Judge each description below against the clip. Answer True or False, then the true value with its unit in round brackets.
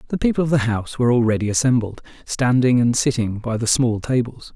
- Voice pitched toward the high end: False (120 Hz)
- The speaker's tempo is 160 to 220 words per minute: True (200 wpm)